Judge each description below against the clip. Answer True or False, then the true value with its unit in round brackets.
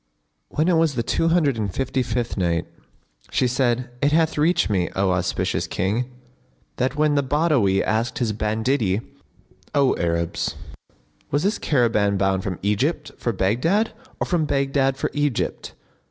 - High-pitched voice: False (125 Hz)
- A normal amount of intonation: False (6.4 semitones)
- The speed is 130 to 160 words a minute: True (155 wpm)